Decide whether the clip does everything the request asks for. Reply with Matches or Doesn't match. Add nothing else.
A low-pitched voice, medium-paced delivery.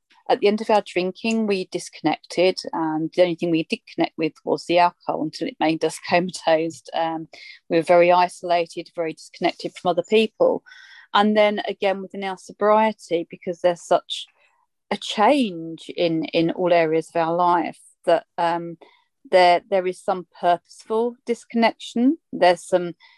Doesn't match